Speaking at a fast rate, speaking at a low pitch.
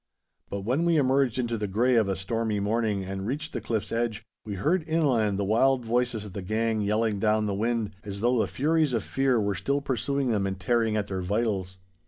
Yes: fast, 220 wpm; low, 115 Hz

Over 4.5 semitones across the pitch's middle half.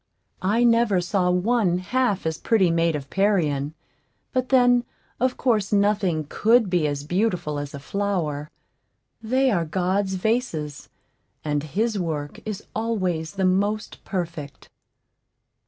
Yes: wide, 5.4 semitones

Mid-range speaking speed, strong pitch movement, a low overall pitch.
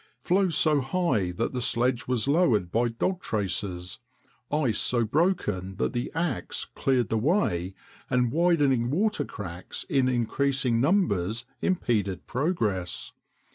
No: slow, 130 wpm; wide, 6.6 semitones; low, 125 Hz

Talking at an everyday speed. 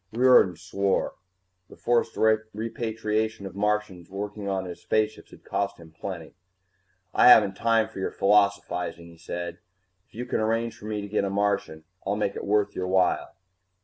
Yes: average, 170 wpm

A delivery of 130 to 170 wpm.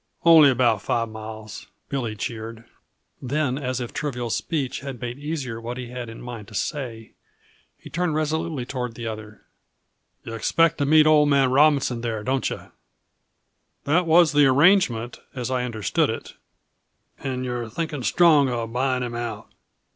Yes: average, 160 wpm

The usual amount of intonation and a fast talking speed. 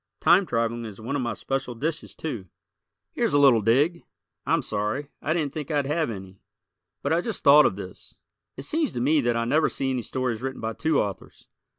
Yes: average, 4.7 semitones; fast, 210 wpm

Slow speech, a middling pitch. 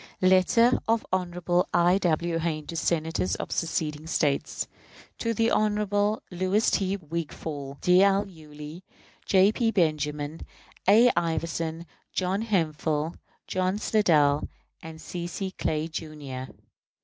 Yes: slow, 120 wpm; medium, 170 Hz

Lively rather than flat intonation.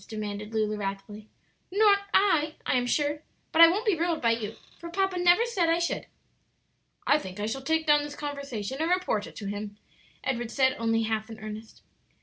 Yes: wide, 7.5 semitones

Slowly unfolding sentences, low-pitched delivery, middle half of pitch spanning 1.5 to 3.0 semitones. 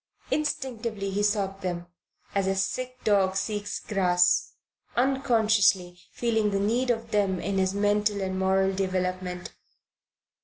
No: slow, 125 wpm; high, 200 Hz; narrow, 2.6 semitones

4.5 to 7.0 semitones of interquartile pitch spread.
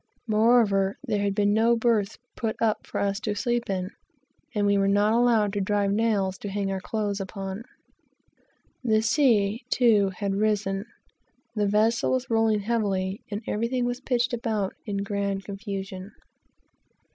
No: narrow, 2.4 semitones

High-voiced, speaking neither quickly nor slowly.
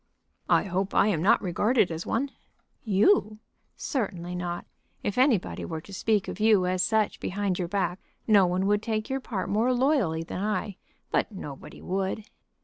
Yes: high, 200 Hz; average, 170 wpm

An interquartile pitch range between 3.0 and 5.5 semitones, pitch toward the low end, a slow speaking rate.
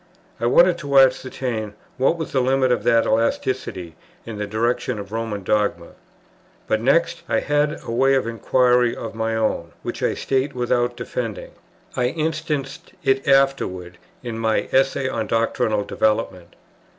No: average, 3.5 semitones; low, 120 Hz; average, 150 wpm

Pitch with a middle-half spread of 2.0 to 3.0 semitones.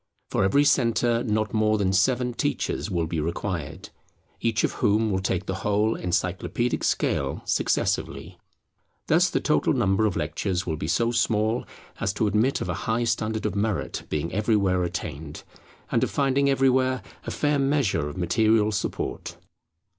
No: average, 4.2 semitones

